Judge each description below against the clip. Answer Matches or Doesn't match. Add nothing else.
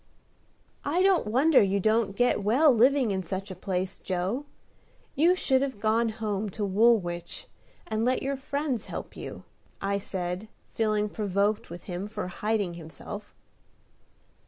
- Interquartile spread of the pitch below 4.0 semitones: Doesn't match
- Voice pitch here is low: Doesn't match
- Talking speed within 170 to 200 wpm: Doesn't match